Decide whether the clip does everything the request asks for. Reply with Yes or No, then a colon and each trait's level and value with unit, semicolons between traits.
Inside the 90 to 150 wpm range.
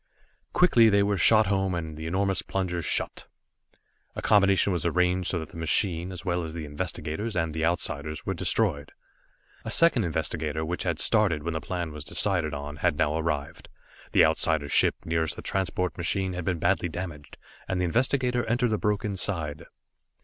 No: average, 180 wpm